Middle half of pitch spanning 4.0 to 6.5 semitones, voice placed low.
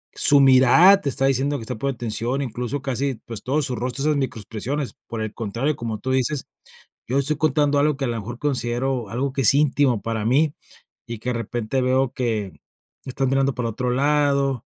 No: average, 2.9 semitones; low, 130 Hz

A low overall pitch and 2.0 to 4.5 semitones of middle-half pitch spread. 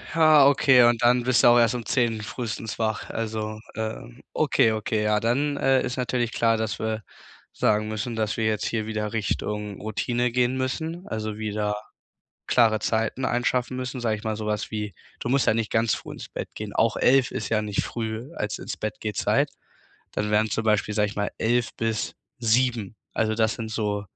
Yes: low, 110 Hz; narrow, 2.3 semitones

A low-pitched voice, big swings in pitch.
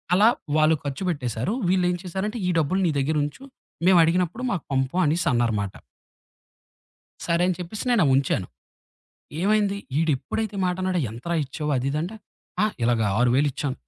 No: medium, 165 Hz; wide, 5.7 semitones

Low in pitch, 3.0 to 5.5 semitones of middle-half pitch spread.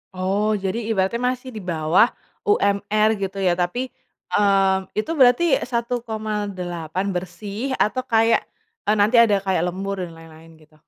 No: high, 200 Hz; average, 3.7 semitones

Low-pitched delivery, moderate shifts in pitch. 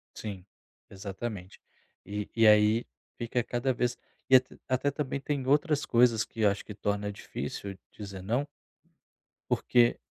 Yes: low, 115 Hz; average, 3.8 semitones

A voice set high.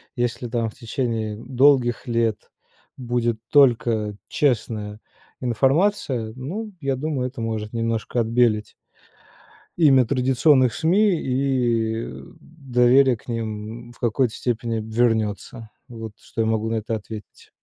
No: low, 120 Hz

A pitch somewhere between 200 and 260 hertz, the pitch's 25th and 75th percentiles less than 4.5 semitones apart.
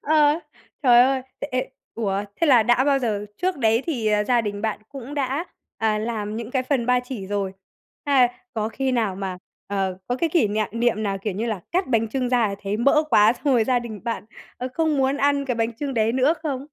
Yes: high, 240 Hz; average, 4.0 semitones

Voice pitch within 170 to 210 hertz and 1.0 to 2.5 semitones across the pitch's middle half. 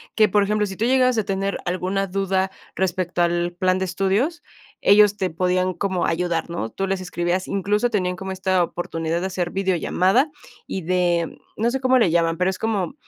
Yes: high, 190 Hz; narrow, 2.2 semitones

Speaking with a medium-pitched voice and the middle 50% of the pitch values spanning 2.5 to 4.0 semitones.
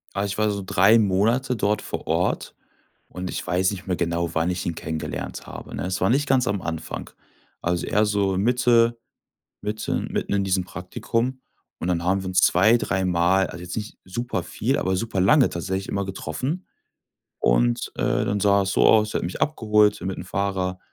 No: very low, 95 Hz; average, 2.9 semitones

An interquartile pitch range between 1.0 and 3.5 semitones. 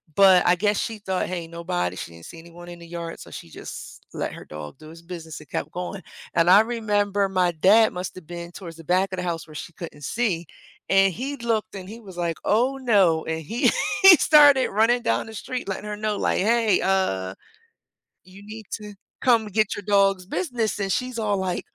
No: average, 4.3 semitones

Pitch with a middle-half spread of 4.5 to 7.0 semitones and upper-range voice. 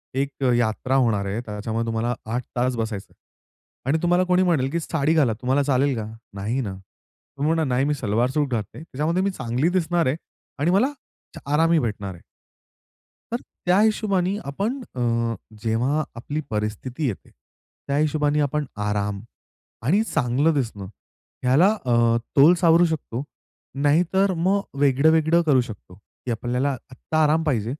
No: wide, 5.6 semitones; medium, 140 Hz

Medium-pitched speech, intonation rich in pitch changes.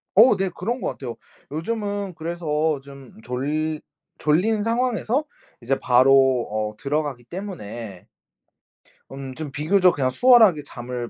Yes: medium, 150 Hz; wide, 7.3 semitones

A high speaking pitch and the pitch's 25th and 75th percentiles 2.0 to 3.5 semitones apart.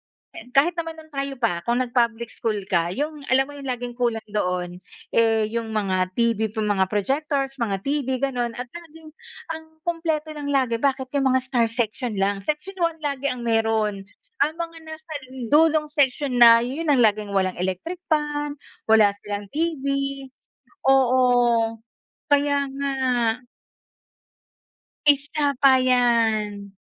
No: very high, 255 Hz; average, 4.7 semitones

